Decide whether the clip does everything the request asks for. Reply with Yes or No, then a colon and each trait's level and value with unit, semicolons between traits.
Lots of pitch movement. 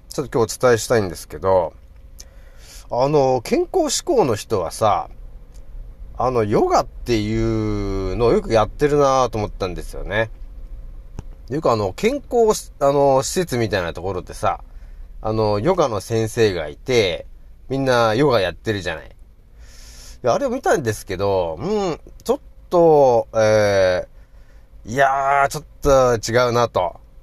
Yes: wide, 6.2 semitones